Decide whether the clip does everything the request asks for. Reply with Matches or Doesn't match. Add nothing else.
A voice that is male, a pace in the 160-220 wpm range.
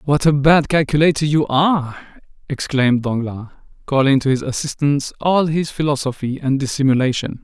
Doesn't match